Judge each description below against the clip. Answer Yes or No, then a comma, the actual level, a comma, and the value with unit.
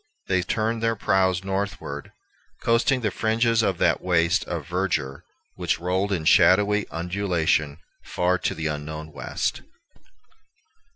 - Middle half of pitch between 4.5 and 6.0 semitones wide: No, average, 3.8 semitones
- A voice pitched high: No, very low, 95 Hz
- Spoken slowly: Yes, slow, 125 wpm